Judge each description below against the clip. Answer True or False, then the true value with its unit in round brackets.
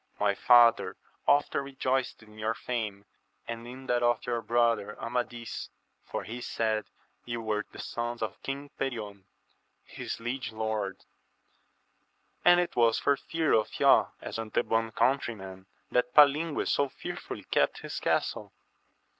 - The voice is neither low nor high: False (120 Hz)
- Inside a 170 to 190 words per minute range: False (140 wpm)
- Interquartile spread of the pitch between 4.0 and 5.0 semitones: False (3.0 semitones)